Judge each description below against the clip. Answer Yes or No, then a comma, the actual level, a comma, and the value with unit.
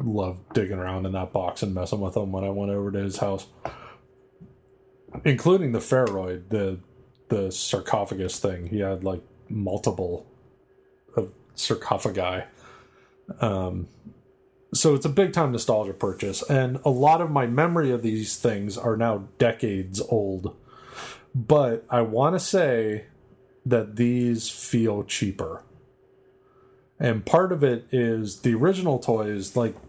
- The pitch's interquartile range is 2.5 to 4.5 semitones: No, average, 4.9 semitones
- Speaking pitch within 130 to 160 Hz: No, low, 115 Hz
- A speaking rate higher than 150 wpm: No, average, 140 wpm